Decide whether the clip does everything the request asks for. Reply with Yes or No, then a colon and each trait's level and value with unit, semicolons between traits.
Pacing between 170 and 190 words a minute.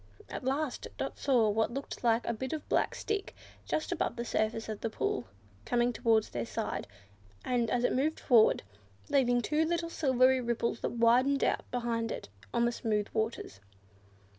Yes: average, 175 wpm